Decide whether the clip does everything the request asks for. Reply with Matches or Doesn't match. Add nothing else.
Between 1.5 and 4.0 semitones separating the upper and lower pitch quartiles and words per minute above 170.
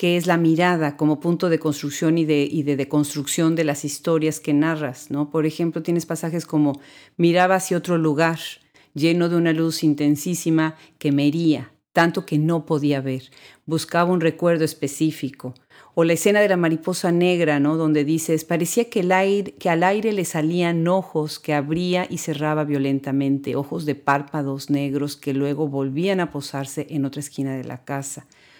Matches